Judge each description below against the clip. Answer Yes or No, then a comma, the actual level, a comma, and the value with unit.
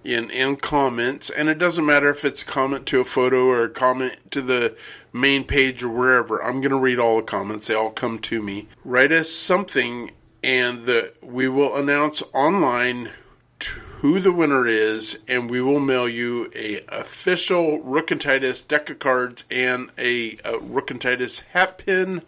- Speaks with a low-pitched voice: Yes, low, 130 Hz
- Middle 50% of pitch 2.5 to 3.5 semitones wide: Yes, average, 2.8 semitones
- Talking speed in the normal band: Yes, average, 185 wpm